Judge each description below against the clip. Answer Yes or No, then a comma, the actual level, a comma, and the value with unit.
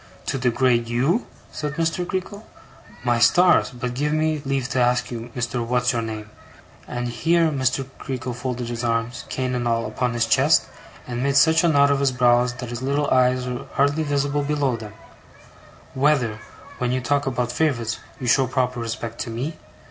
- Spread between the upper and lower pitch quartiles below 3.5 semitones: Yes, average, 2.9 semitones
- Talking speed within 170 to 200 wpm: Yes, average, 185 wpm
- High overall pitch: No, low, 125 Hz